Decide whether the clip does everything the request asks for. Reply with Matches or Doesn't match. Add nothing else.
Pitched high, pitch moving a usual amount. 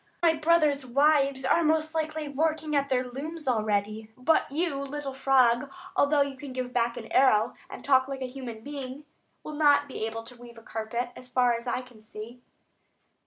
Matches